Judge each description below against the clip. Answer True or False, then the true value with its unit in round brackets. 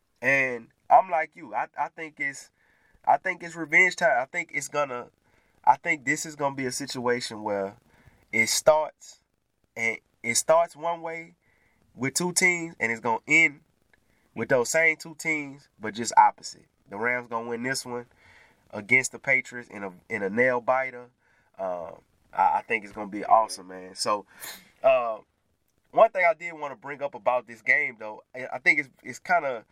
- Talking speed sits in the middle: True (185 wpm)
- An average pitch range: False (5.7 semitones)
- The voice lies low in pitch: True (130 Hz)